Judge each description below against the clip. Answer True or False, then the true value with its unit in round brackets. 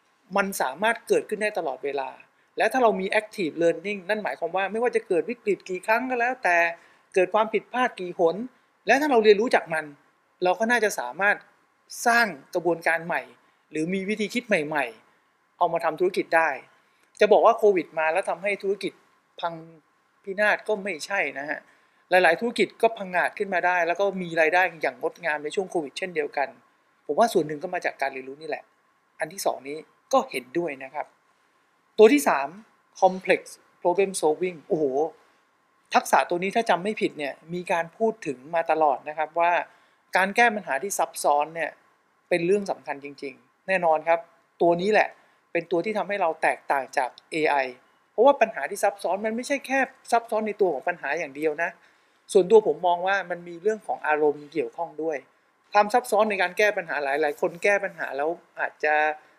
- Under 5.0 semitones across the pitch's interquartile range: False (5.3 semitones)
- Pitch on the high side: True (195 Hz)